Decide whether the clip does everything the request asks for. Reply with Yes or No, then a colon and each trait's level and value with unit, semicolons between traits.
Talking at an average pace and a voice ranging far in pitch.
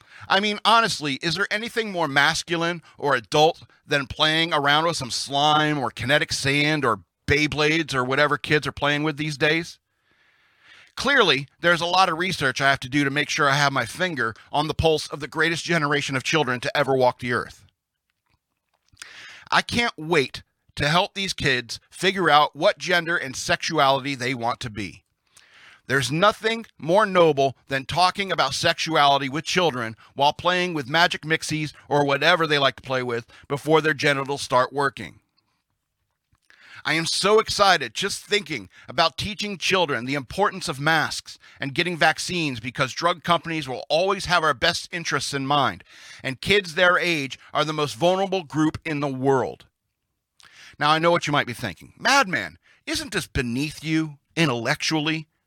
No: average, 170 wpm; average, 3.9 semitones